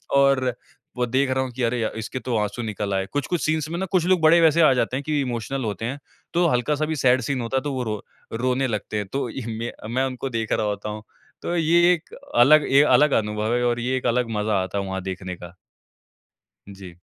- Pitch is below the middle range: Yes, low, 125 Hz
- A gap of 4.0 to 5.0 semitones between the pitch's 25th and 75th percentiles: Yes, average, 4.7 semitones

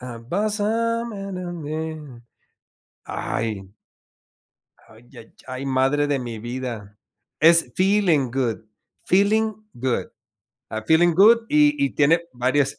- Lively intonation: Yes, wide, 7.8 semitones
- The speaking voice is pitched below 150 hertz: No, medium, 155 Hz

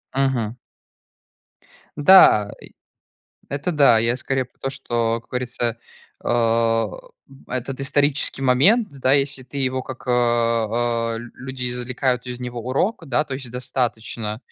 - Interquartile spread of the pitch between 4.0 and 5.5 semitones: No, narrow, 2.4 semitones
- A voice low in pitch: Yes, low, 125 Hz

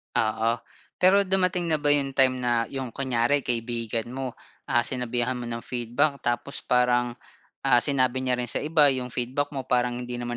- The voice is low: Yes, low, 125 Hz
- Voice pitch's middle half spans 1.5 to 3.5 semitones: Yes, narrow, 2.5 semitones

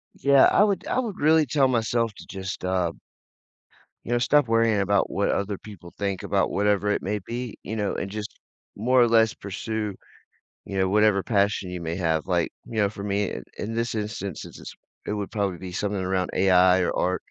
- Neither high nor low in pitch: No, low, 105 Hz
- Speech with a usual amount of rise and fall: Yes, average, 3.2 semitones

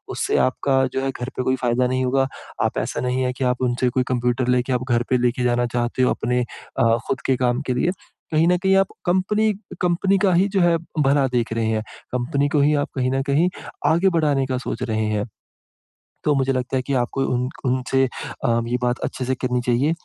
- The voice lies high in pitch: No, low, 130 Hz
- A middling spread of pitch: No, narrow, 2.3 semitones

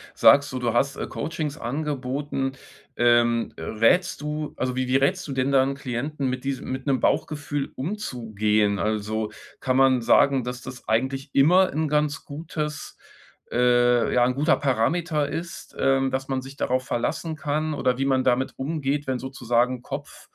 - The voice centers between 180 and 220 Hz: No, low, 135 Hz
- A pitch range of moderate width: Yes, average, 3.0 semitones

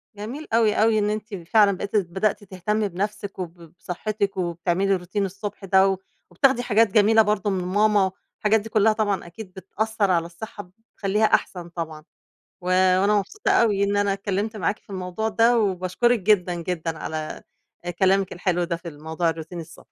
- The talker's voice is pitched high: Yes, high, 195 Hz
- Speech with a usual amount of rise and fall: Yes, average, 3.0 semitones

